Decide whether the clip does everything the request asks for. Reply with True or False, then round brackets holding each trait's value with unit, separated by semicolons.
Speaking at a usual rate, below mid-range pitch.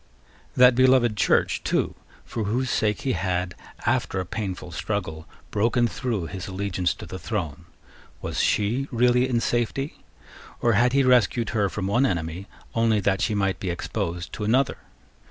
True (160 wpm; 105 Hz)